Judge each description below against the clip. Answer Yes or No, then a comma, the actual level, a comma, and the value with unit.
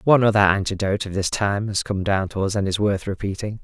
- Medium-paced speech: No, fast, 250 wpm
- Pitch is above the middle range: No, low, 100 Hz